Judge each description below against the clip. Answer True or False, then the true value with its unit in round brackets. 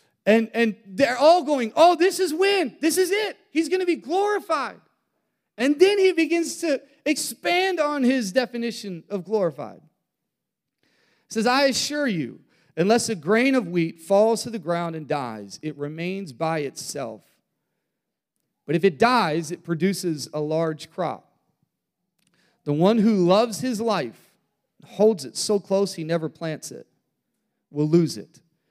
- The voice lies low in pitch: False (215 Hz)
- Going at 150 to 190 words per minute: True (155 wpm)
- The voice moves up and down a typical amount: False (8.6 semitones)